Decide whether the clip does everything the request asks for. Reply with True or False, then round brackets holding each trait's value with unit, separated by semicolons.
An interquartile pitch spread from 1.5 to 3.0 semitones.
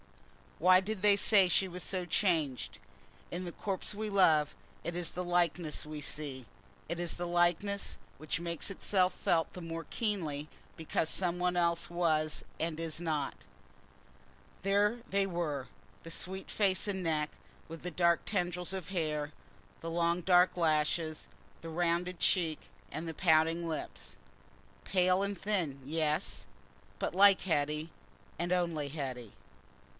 True (2.7 semitones)